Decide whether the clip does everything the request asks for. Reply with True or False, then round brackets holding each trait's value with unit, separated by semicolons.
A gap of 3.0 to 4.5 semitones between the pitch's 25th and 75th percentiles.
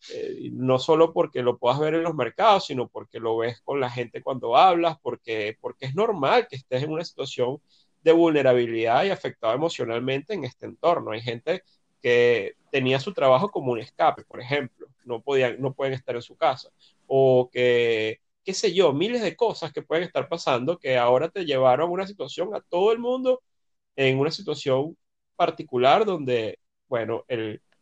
False (5.5 semitones)